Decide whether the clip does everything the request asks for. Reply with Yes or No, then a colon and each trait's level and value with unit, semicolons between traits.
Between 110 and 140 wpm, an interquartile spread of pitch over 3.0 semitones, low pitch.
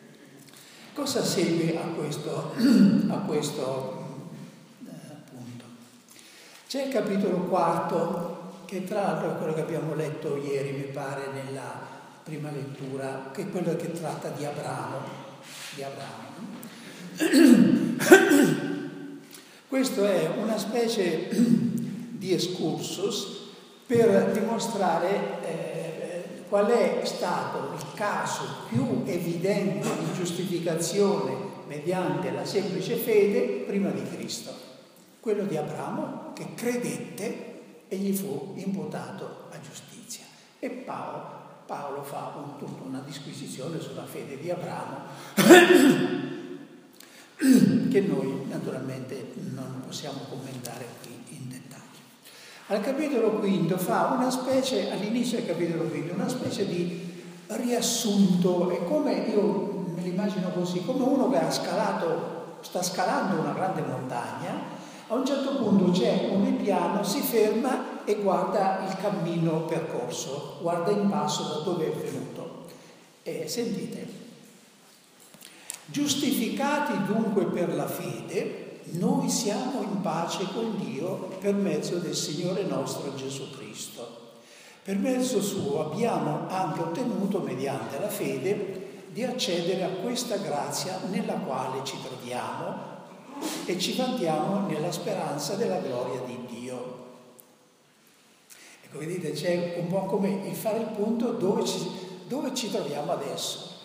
No: average, 120 wpm; wide, 5.5 semitones; high, 190 Hz